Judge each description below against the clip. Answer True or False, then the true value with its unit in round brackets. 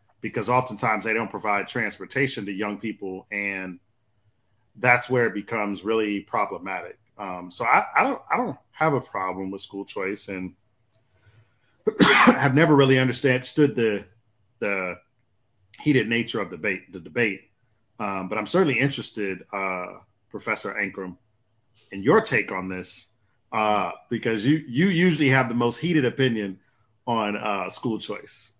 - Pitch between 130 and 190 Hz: False (110 Hz)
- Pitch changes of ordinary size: True (3.4 semitones)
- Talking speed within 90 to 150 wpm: True (145 wpm)